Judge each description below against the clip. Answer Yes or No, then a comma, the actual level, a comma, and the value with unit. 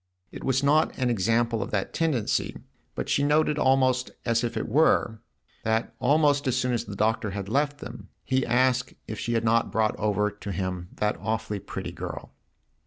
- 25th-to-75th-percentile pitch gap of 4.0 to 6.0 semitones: No, average, 3.6 semitones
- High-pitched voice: No, low, 115 Hz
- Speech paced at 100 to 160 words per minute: No, average, 185 wpm